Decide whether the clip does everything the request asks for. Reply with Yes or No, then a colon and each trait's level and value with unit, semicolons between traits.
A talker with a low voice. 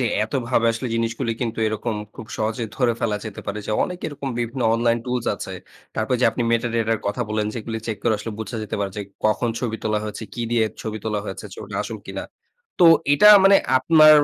Yes: low, 115 Hz